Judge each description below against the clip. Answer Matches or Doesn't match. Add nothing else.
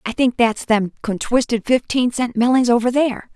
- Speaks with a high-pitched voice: Matches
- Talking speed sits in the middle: Matches